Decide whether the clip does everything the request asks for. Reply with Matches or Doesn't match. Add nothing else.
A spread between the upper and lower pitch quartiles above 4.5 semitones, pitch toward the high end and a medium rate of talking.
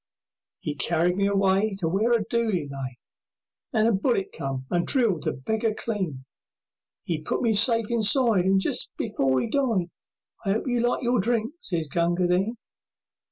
Matches